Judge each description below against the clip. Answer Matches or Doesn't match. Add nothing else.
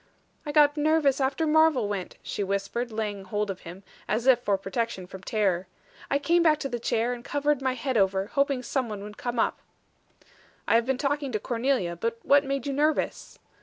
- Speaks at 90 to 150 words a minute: Doesn't match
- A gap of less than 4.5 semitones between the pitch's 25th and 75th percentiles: Doesn't match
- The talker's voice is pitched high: Matches